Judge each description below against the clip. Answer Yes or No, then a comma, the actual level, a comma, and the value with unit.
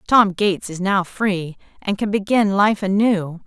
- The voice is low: No, high, 195 Hz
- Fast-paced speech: No, average, 175 wpm